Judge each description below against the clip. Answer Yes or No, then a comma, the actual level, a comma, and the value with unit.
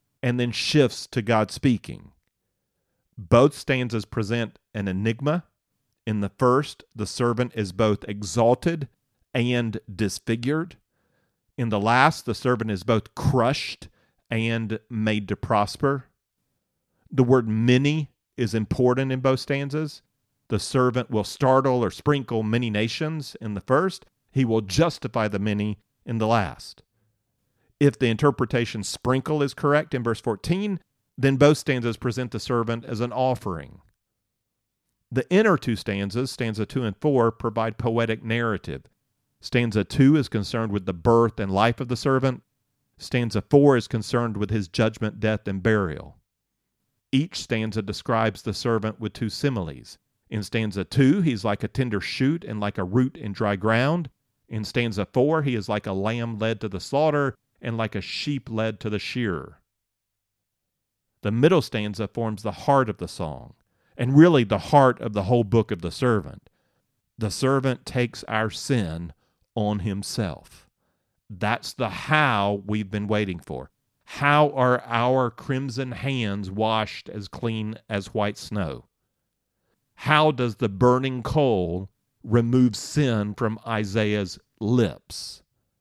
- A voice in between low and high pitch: No, low, 115 Hz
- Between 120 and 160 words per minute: Yes, average, 145 wpm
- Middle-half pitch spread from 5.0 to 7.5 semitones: No, average, 3.6 semitones